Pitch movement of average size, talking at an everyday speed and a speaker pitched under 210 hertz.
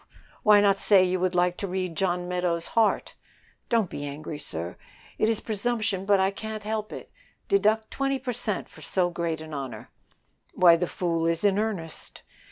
Yes: average, 4.1 semitones; average, 180 wpm; medium, 185 Hz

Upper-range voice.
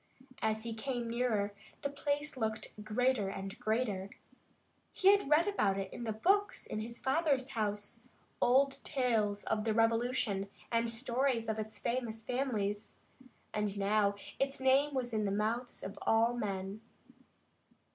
Yes: high, 230 Hz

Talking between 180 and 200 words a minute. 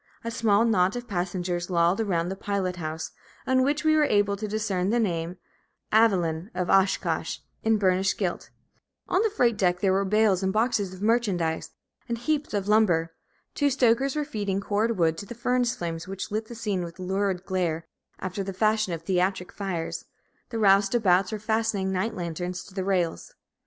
Yes: average, 185 wpm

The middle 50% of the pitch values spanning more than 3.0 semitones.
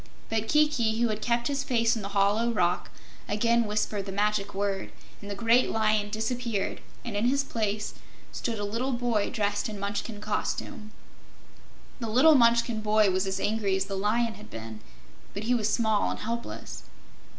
No: narrow, 2.5 semitones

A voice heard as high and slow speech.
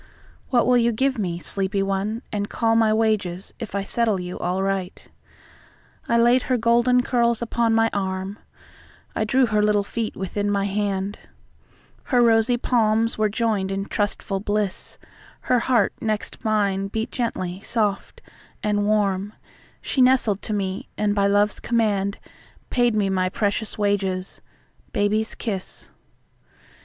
Yes: high, 210 Hz; slow, 125 wpm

